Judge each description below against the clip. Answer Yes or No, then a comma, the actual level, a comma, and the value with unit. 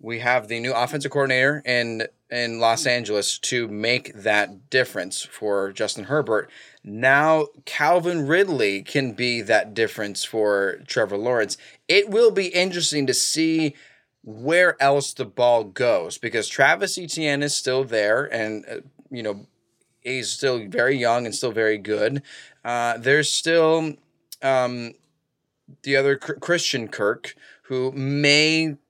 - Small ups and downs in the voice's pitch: No, average, 4.3 semitones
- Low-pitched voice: Yes, low, 130 Hz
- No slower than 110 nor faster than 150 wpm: Yes, average, 140 wpm